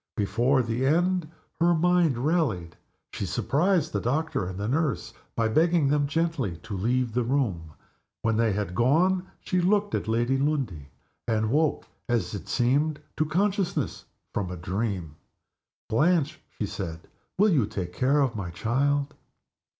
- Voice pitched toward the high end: No, low, 130 Hz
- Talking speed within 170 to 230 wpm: No, average, 150 wpm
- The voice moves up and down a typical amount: No, wide, 7.0 semitones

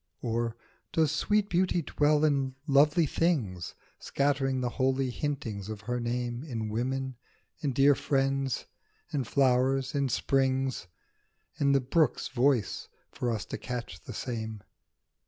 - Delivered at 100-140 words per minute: Yes, slow, 135 wpm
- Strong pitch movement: No, average, 3.0 semitones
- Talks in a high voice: No, low, 130 Hz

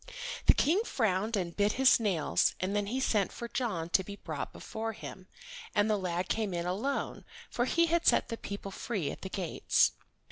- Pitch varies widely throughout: No, average, 4.1 semitones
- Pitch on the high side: Yes, high, 205 Hz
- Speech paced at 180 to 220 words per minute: Yes, average, 200 wpm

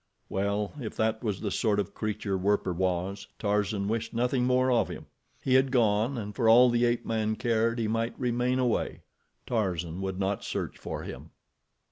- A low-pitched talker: Yes, low, 110 Hz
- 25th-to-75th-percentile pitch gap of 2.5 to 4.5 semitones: Yes, average, 3.0 semitones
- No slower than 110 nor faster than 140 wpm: No, average, 175 wpm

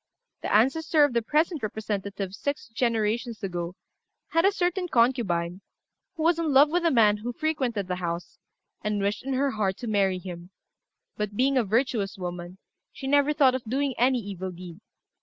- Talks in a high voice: Yes, high, 230 Hz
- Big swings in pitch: Yes, wide, 6.1 semitones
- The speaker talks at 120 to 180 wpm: Yes, average, 175 wpm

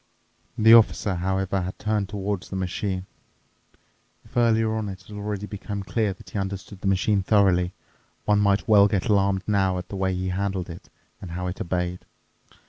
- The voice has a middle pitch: No, low, 100 Hz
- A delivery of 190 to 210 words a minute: No, average, 180 wpm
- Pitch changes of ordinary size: No, narrow, 1.8 semitones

